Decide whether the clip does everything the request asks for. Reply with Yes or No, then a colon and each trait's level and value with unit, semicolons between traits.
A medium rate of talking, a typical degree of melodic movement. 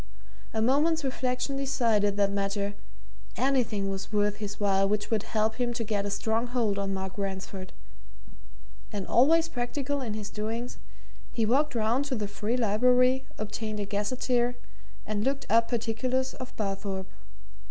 Yes: average, 155 wpm; average, 3.7 semitones